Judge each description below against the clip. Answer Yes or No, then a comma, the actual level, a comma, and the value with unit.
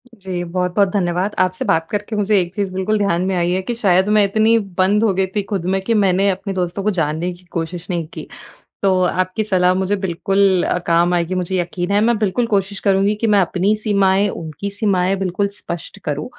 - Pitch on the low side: No, high, 190 Hz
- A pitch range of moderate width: No, narrow, 2.2 semitones